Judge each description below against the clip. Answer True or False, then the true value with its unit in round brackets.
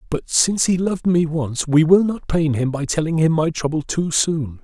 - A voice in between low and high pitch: True (160 Hz)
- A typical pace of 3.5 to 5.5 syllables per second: True (5.0 syllables/s)